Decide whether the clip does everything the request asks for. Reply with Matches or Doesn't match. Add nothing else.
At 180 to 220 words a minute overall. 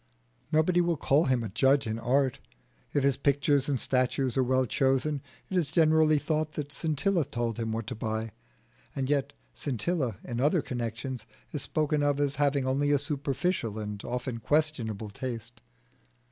Doesn't match